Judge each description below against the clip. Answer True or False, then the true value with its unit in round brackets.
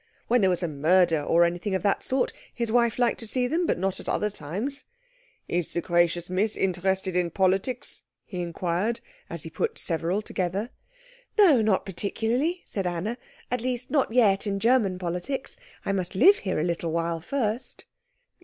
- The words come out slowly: False (180 wpm)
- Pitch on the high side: True (195 Hz)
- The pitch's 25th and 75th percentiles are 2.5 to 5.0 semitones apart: False (5.4 semitones)